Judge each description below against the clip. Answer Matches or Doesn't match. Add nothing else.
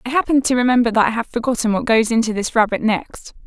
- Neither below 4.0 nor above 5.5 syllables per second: Doesn't match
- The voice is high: Matches